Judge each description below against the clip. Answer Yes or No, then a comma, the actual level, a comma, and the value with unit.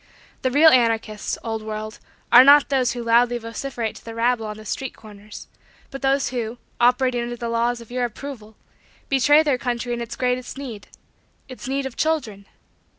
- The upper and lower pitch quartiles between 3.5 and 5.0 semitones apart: No, narrow, 2.6 semitones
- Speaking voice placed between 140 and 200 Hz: No, high, 240 Hz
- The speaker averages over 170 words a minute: Yes, average, 180 wpm